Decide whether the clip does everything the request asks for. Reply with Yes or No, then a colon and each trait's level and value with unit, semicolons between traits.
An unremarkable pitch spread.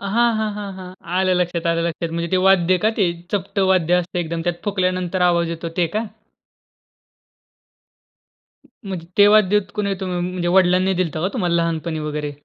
No: narrow, 2.1 semitones